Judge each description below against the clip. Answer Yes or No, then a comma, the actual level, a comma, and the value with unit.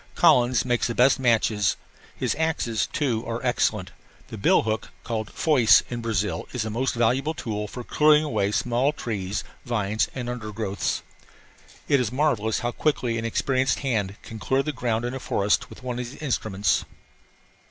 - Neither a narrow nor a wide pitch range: Yes, average, 3.1 semitones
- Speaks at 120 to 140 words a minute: No, average, 175 wpm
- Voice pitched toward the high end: No, low, 120 Hz